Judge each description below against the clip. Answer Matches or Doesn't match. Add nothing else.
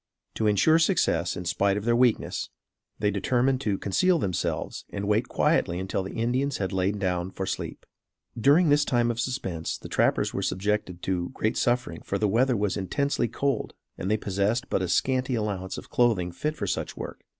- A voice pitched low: Matches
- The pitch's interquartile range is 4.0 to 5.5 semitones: Matches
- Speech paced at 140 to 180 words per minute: Doesn't match